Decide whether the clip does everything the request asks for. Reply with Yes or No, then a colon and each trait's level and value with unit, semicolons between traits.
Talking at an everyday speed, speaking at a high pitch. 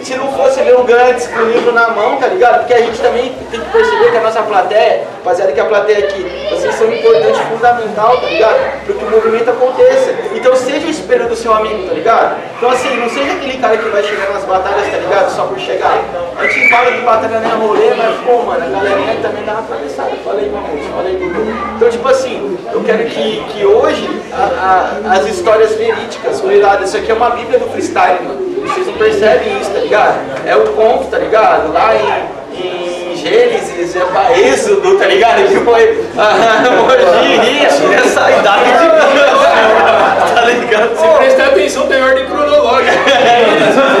No: fast, 205 wpm; high, 245 Hz